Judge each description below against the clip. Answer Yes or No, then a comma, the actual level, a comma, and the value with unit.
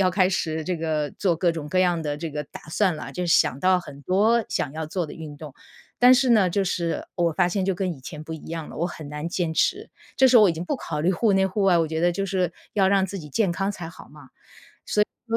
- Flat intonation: No, average, 3.4 semitones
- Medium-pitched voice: Yes, medium, 175 Hz